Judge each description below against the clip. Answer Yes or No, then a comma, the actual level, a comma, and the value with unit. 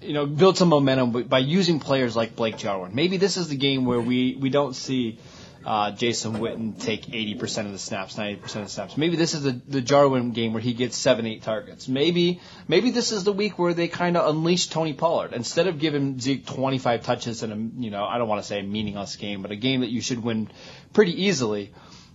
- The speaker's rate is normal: No, fast, 240 wpm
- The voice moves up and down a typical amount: No, wide, 5.8 semitones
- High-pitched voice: No, low, 130 Hz